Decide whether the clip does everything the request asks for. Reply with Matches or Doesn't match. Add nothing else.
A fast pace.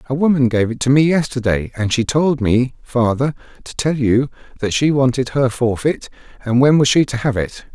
Matches